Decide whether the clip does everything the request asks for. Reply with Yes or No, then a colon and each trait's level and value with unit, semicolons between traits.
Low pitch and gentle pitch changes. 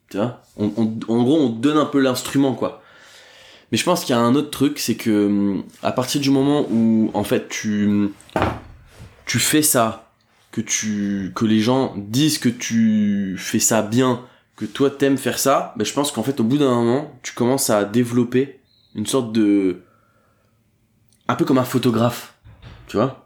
No: low, 115 Hz; average, 3.5 semitones